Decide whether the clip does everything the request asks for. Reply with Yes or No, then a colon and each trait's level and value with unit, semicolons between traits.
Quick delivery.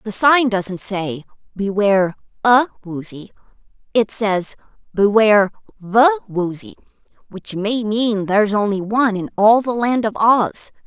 No: slow, 135 wpm